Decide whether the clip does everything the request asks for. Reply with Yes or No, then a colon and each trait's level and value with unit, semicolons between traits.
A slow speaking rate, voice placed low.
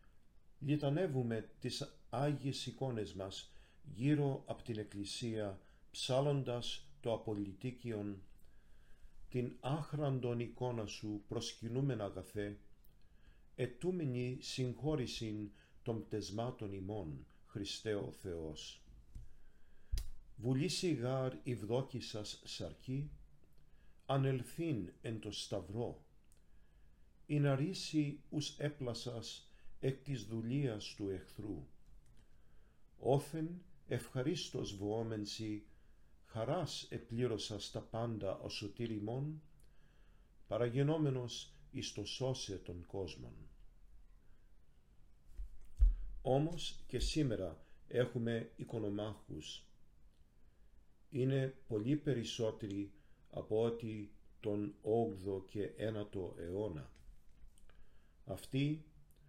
Yes: slow, 75 wpm; low, 115 Hz